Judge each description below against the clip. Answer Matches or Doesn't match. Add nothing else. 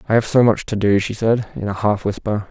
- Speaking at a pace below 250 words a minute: Doesn't match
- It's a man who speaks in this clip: Matches